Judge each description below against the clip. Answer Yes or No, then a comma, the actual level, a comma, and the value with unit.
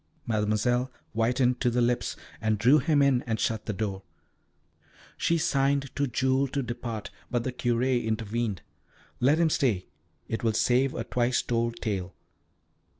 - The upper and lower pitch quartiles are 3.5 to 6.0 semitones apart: No, average, 2.9 semitones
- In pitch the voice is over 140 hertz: No, low, 120 Hz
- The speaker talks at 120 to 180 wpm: Yes, average, 150 wpm